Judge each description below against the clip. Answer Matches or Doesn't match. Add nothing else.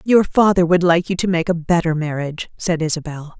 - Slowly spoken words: Doesn't match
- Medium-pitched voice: Matches